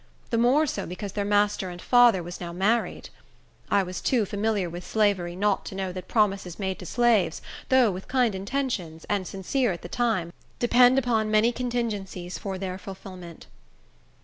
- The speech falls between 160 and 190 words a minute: Yes, average, 175 wpm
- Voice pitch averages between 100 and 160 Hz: No, high, 200 Hz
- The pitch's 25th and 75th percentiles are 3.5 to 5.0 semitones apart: Yes, average, 4.2 semitones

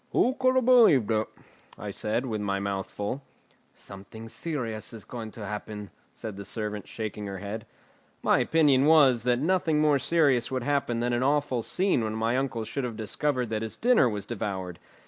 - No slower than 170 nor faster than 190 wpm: Yes, average, 185 wpm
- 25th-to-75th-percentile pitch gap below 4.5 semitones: No, average, 4.9 semitones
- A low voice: Yes, low, 120 Hz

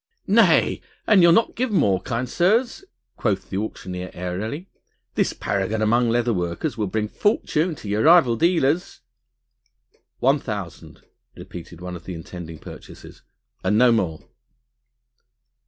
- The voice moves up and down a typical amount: No, wide, 8.9 semitones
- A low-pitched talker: Yes, low, 110 Hz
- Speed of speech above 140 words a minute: No, slow, 135 wpm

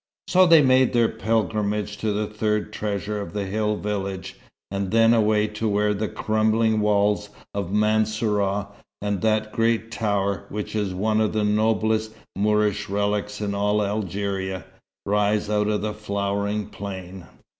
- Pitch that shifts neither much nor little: No, narrow, 1.2 semitones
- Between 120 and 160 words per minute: Yes, average, 150 wpm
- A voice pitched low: Yes, low, 105 Hz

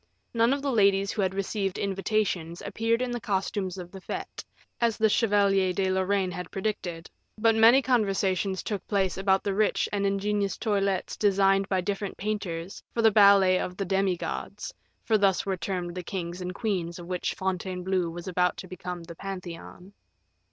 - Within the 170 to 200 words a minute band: Yes, average, 180 wpm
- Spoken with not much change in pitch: Yes, narrow, 2.1 semitones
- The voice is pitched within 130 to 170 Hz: No, high, 195 Hz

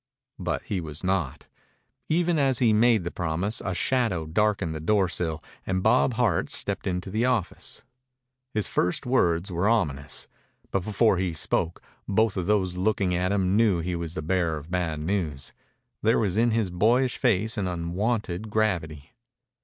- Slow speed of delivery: No, average, 165 wpm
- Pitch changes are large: No, average, 4.1 semitones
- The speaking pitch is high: No, very low, 95 Hz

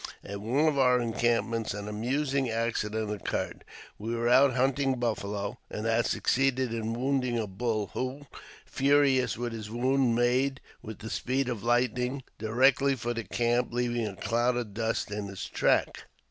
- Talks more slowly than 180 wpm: Yes, average, 160 wpm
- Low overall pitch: Yes, low, 120 Hz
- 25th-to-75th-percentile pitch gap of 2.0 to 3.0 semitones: Yes, average, 2.7 semitones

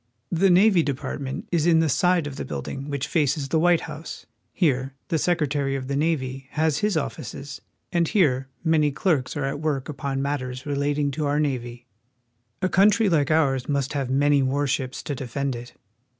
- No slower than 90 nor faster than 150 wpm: No, average, 180 wpm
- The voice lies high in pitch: No, medium, 145 Hz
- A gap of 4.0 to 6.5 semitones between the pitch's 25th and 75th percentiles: No, average, 3.1 semitones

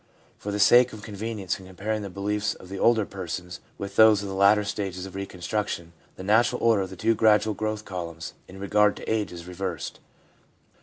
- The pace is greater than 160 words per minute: Yes, average, 200 wpm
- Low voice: Yes, low, 100 Hz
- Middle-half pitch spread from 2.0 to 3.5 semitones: Yes, narrow, 2.4 semitones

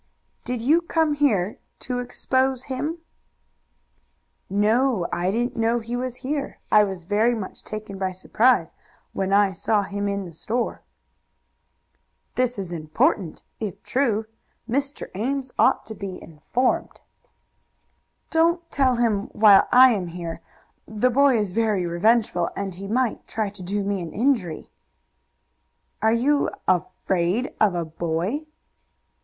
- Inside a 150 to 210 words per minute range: No, slow, 135 wpm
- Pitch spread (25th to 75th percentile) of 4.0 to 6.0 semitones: Yes, average, 5.0 semitones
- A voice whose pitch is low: No, high, 215 Hz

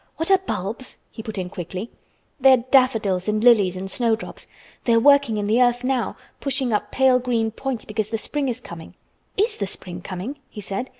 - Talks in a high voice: Yes, high, 230 Hz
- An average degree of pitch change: Yes, average, 4.2 semitones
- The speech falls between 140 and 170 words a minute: No, average, 195 wpm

